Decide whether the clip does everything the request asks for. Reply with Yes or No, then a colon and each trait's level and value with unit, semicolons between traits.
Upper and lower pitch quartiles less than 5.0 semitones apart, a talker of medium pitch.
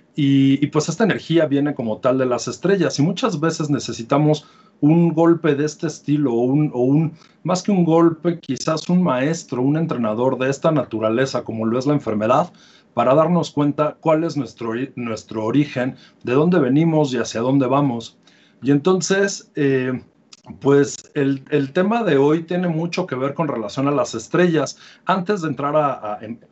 Yes: average, 4.2 semitones; medium, 145 Hz